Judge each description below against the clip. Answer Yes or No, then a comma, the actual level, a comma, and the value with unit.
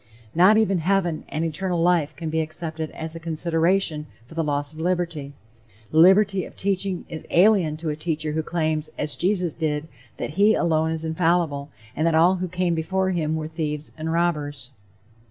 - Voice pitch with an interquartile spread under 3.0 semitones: Yes, narrow, 2.4 semitones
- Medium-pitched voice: Yes, medium, 160 Hz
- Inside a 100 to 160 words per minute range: No, average, 185 wpm